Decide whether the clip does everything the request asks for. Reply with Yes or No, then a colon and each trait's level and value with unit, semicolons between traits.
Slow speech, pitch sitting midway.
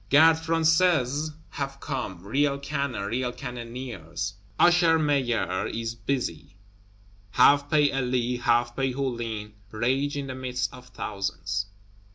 No: slow, 120 wpm; low, 125 Hz